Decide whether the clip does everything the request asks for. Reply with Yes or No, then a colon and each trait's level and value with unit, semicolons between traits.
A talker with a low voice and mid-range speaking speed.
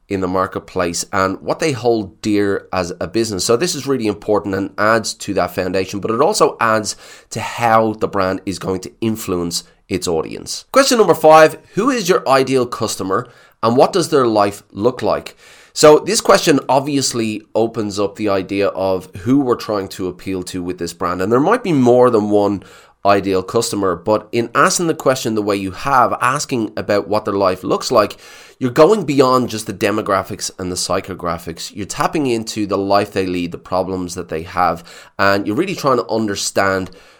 Yes: low, 105 Hz; average, 195 wpm